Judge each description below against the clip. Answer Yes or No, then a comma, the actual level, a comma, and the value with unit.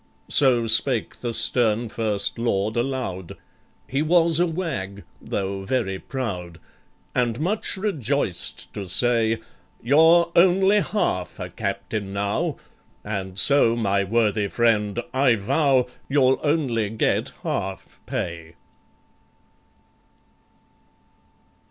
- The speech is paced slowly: Yes, slow, 100 wpm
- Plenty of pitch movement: Yes, wide, 5.9 semitones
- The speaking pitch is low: Yes, low, 115 Hz